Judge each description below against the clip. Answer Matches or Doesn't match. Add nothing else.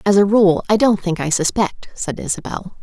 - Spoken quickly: Matches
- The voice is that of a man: Doesn't match